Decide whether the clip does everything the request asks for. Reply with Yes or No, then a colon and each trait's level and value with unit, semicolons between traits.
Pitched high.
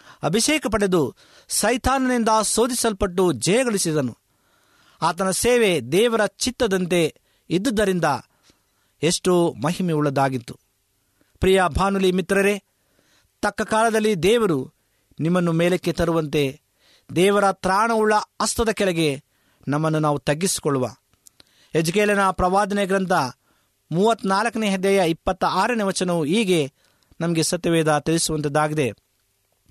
No: medium, 180 Hz